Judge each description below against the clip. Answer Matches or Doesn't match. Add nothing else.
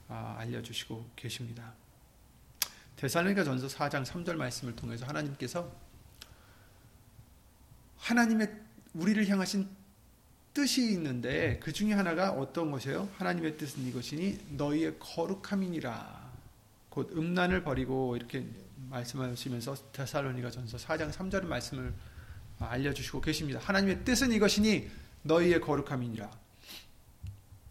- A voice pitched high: Doesn't match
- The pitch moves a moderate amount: Doesn't match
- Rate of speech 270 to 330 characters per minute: Matches